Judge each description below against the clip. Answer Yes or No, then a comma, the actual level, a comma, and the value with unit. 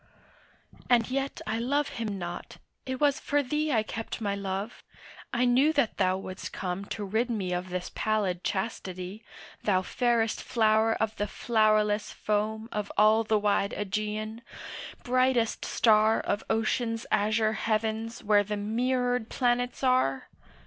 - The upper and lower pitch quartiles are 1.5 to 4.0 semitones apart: Yes, average, 2.7 semitones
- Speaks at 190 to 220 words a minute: No, average, 145 wpm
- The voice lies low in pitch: No, high, 220 Hz